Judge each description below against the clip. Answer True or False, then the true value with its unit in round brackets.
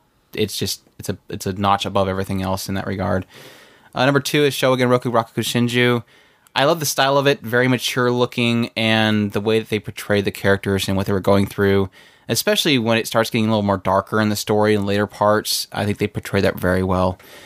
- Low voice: True (105 Hz)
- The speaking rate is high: True (225 wpm)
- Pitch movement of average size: True (3.5 semitones)